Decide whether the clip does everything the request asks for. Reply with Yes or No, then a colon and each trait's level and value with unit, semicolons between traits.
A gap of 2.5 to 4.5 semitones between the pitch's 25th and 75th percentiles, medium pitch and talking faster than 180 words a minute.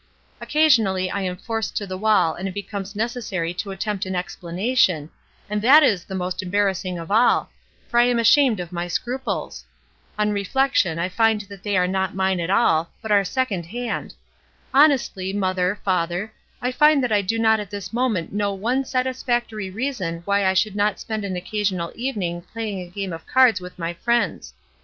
No: average, 3.8 semitones; high, 200 Hz; average, 195 wpm